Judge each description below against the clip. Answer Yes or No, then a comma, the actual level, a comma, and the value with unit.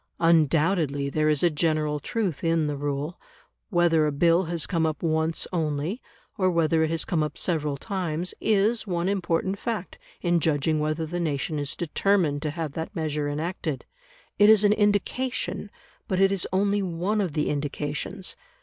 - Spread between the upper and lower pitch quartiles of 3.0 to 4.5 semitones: Yes, average, 3.7 semitones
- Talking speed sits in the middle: Yes, average, 170 wpm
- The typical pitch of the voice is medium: Yes, medium, 165 Hz